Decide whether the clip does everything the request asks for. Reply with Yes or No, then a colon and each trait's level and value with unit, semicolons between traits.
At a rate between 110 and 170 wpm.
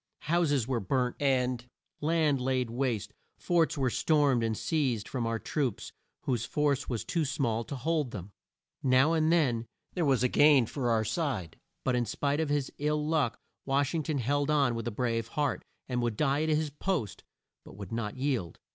No: average, 190 wpm